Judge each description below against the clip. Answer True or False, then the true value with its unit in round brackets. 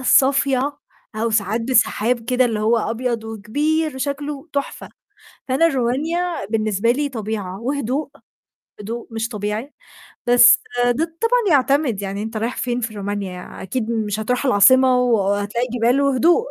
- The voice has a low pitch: False (240 Hz)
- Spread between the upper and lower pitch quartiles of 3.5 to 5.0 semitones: True (4.2 semitones)